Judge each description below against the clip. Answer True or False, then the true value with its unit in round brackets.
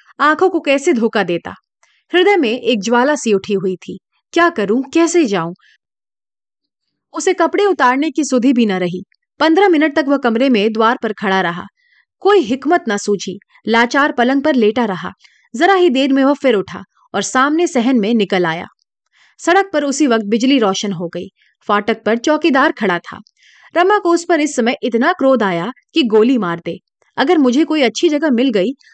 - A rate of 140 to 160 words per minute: False (185 wpm)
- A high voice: True (260 Hz)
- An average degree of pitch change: False (7.2 semitones)